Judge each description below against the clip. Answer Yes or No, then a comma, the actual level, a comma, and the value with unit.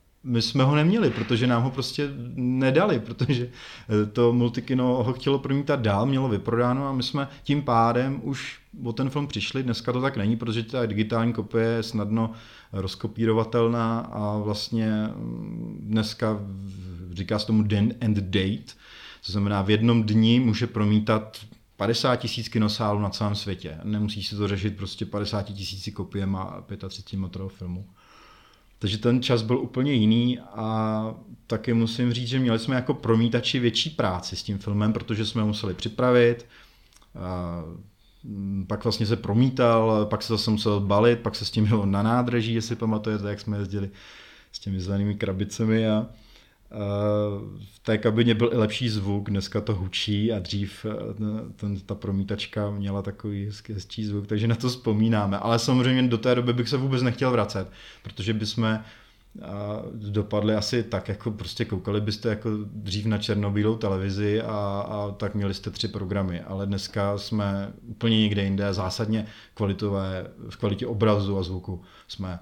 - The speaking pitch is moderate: No, low, 110 Hz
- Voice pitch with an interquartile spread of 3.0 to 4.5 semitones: No, narrow, 2.6 semitones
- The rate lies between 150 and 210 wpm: Yes, average, 155 wpm